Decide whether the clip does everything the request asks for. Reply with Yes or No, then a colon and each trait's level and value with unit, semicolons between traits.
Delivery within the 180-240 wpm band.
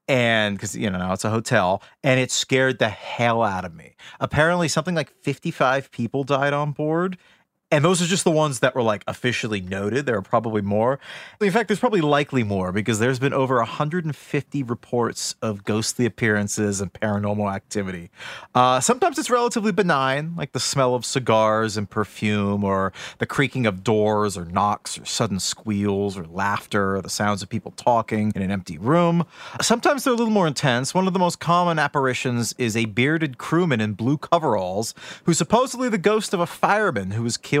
Yes: average, 190 wpm